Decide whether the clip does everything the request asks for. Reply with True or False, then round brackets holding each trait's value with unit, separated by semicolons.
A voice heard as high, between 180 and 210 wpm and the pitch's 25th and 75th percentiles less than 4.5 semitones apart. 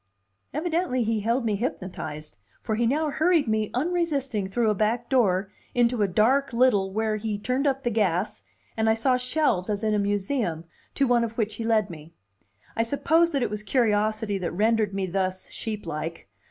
True (220 Hz; 190 wpm; 3.9 semitones)